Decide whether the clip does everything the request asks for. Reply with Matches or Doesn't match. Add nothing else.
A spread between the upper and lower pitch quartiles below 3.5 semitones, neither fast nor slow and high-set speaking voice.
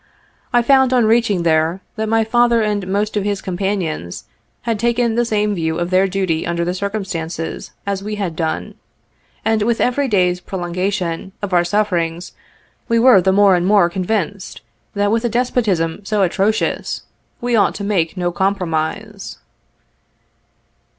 Doesn't match